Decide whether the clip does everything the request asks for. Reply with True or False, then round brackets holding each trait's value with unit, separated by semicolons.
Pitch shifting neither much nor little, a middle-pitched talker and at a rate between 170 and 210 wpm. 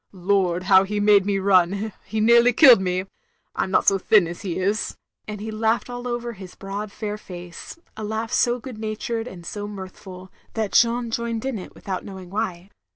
False (3.1 semitones; 205 Hz; 205 wpm)